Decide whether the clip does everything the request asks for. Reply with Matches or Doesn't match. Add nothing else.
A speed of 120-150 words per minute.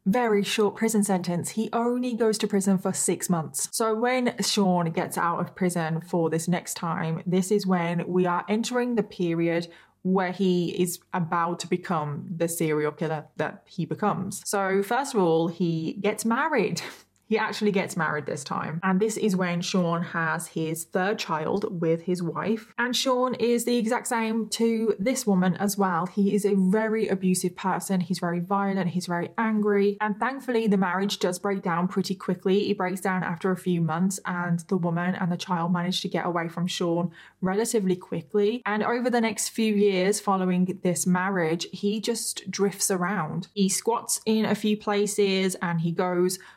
Doesn't match